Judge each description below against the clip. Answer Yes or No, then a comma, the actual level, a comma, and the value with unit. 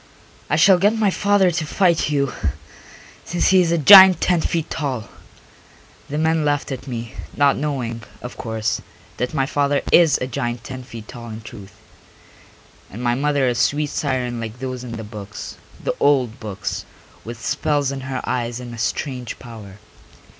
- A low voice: Yes, low, 130 Hz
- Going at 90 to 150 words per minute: No, average, 175 wpm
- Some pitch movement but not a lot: Yes, average, 4.3 semitones